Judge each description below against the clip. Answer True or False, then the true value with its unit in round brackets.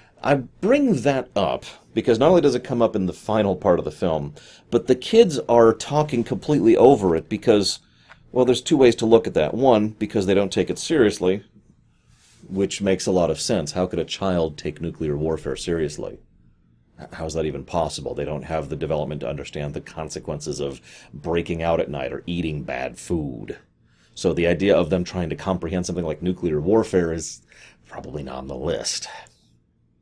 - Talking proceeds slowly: False (195 wpm)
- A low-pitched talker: True (90 Hz)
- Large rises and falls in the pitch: True (5.8 semitones)